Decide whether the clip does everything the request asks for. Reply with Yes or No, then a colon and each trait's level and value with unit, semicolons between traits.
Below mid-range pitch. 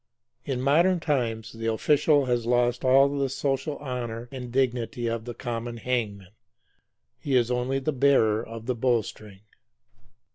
Yes: low, 125 Hz